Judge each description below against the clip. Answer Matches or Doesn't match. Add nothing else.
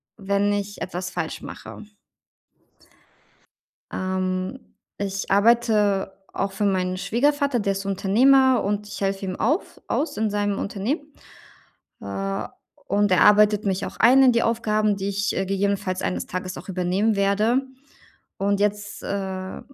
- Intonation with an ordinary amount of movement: Doesn't match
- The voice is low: Doesn't match